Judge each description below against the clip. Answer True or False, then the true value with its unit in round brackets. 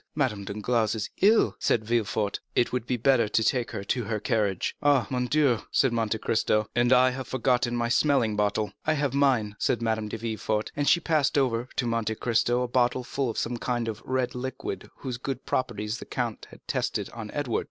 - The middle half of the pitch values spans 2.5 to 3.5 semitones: True (2.9 semitones)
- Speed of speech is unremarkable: False (210 wpm)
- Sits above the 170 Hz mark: False (120 Hz)